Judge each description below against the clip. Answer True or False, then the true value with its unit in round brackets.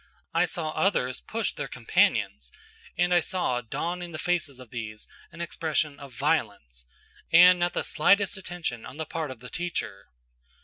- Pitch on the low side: False (160 Hz)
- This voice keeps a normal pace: True (170 wpm)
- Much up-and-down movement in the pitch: True (5.8 semitones)